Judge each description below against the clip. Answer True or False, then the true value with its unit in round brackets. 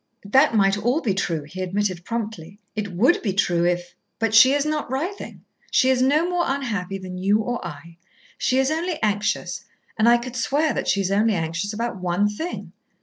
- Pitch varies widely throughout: True (5.9 semitones)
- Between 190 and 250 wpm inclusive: True (200 wpm)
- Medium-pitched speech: False (210 Hz)